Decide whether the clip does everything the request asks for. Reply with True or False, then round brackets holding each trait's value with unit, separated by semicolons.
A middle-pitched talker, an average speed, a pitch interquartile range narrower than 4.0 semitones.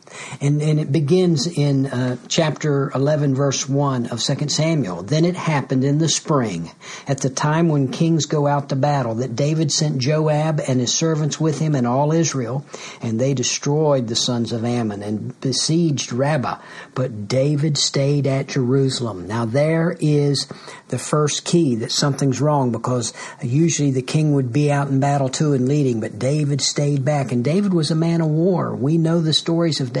True (145 Hz; 185 wpm; 2.9 semitones)